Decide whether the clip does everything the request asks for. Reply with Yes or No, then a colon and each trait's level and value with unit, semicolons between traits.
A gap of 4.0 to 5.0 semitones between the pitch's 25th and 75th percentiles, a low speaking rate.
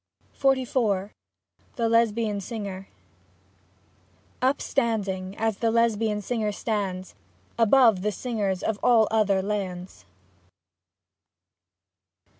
No: average, 2.8 semitones; slow, 80 wpm